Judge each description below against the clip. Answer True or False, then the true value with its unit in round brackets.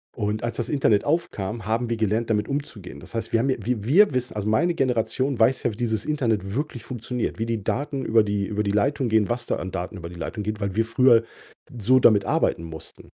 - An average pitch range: True (3.4 semitones)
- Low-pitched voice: True (115 Hz)